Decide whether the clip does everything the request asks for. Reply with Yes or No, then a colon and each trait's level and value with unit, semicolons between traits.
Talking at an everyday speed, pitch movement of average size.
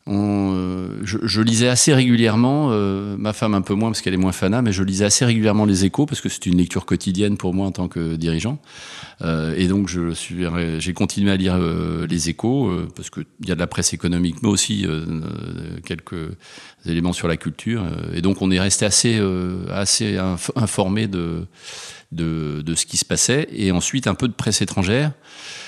Yes: average, 205 wpm; average, 3.6 semitones